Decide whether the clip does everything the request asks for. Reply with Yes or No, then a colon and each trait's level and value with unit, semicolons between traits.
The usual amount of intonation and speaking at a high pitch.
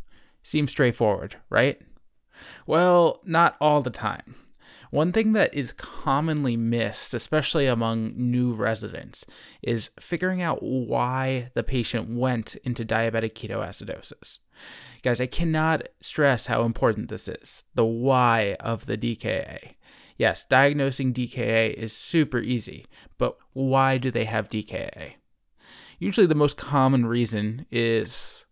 No: average, 3.6 semitones; low, 125 Hz